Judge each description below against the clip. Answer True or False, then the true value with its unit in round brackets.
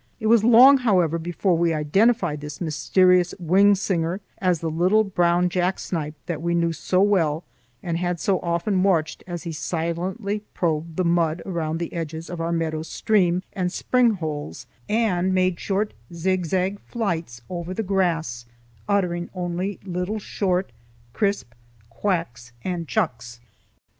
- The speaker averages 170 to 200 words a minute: False (150 wpm)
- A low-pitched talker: False (175 Hz)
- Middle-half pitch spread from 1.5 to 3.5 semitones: True (2.7 semitones)